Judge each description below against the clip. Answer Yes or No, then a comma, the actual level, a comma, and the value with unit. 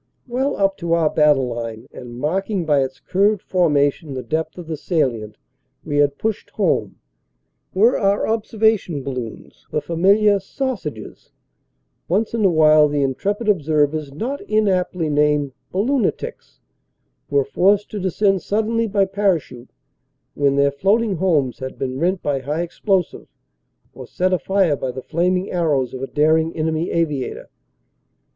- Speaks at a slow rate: No, average, 150 wpm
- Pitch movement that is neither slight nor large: No, wide, 5.7 semitones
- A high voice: No, medium, 165 Hz